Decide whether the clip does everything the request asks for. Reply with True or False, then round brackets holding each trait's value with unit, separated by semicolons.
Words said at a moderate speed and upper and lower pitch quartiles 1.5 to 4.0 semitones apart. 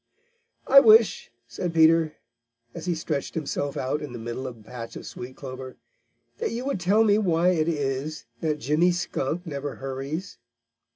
False (170 wpm; 4.8 semitones)